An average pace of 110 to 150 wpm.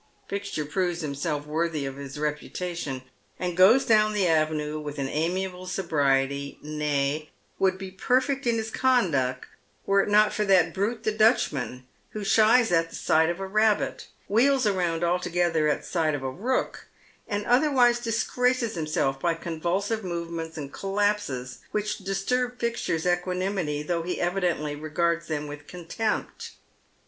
Yes: average, 145 wpm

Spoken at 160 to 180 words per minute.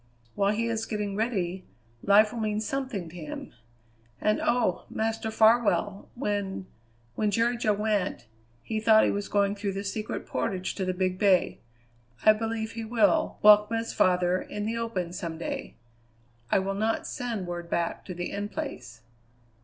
Yes: average, 170 wpm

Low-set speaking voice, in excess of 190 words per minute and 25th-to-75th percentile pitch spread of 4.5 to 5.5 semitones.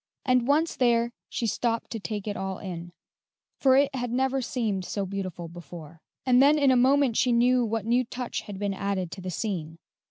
No: high, 230 Hz; average, 200 wpm; average, 4.8 semitones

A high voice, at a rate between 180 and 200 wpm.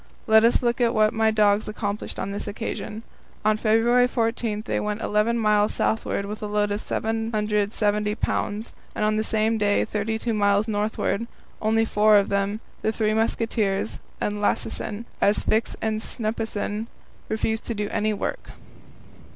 No: high, 215 Hz; average, 160 wpm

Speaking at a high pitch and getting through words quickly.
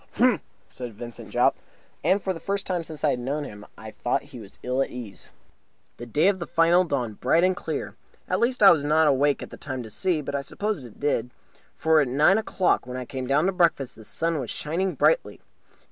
No: medium, 150 Hz; fast, 235 wpm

